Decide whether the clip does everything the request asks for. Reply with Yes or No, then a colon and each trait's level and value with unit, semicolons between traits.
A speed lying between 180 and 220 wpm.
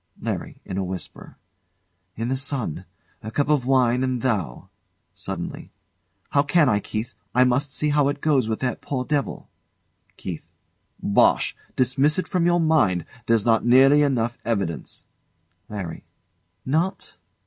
No: average, 145 wpm